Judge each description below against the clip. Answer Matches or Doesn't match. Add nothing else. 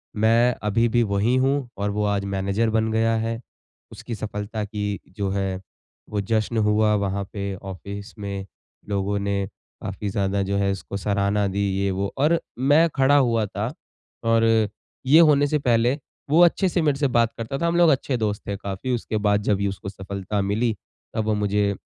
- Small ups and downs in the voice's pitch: Doesn't match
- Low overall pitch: Matches